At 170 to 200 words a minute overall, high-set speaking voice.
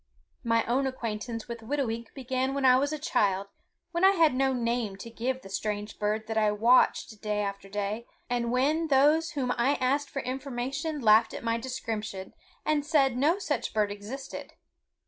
Yes: average, 180 wpm; high, 245 Hz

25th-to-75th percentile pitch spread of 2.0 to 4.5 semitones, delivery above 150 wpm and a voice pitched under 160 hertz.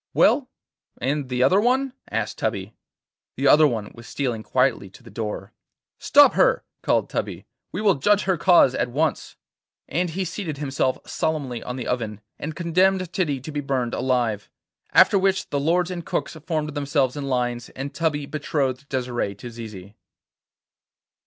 No: average, 5.1 semitones; average, 165 wpm; medium, 140 Hz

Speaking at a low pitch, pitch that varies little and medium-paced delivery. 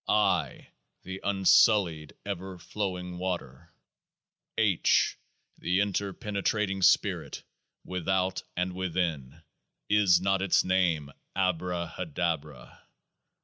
No: very low, 90 Hz; narrow, 2.3 semitones; slow, 80 wpm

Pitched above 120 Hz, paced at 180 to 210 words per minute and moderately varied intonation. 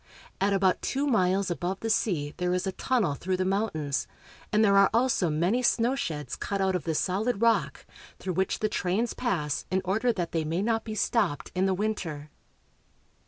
Yes: high, 190 Hz; average, 190 wpm; average, 3.8 semitones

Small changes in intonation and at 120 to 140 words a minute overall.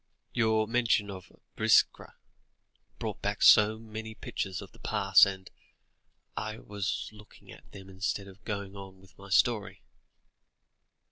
Yes: narrow, 2.0 semitones; slow, 135 wpm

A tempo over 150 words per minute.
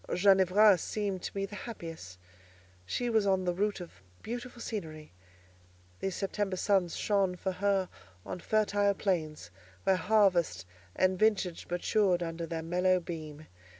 No: average, 140 wpm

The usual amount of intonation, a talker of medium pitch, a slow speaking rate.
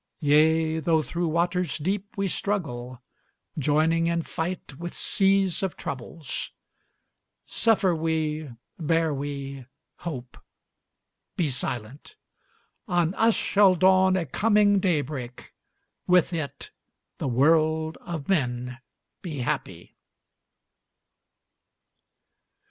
Yes: average, 4.1 semitones; medium, 160 Hz; slow, 95 wpm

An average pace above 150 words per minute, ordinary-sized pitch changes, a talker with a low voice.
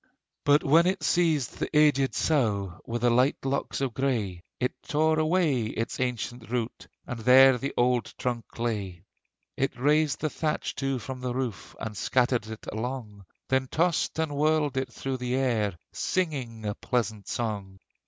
Yes: average, 165 wpm; average, 4.1 semitones; low, 125 Hz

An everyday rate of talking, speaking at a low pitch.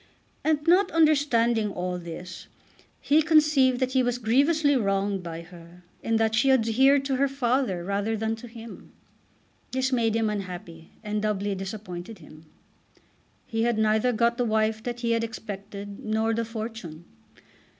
No: average, 155 wpm; high, 225 Hz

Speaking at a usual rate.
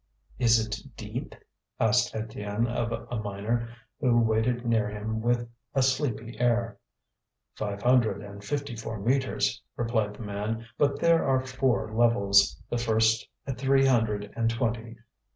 Yes: average, 145 wpm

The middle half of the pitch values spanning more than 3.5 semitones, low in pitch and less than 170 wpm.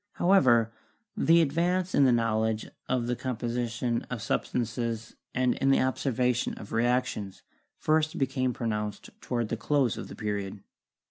No: average, 2.7 semitones; low, 120 Hz; average, 140 wpm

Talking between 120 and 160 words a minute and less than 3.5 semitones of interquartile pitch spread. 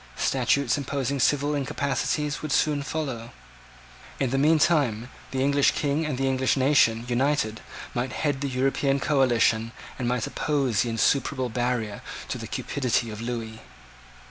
Yes: average, 145 wpm; average, 2.9 semitones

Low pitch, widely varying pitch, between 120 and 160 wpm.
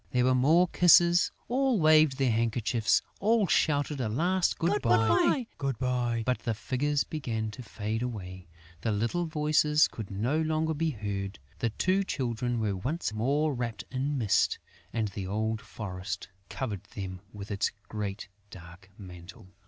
Yes: low, 120 Hz; wide, 6.3 semitones; average, 150 wpm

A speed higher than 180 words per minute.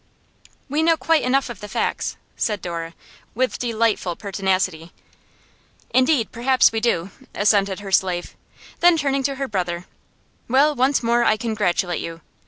No: average, 145 wpm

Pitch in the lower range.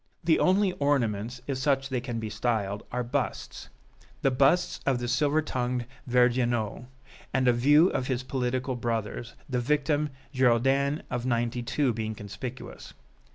Yes: low, 125 Hz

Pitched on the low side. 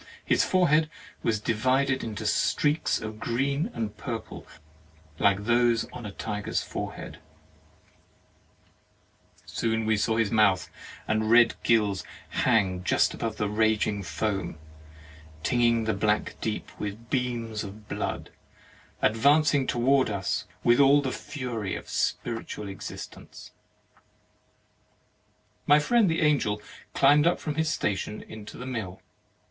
Yes: low, 115 Hz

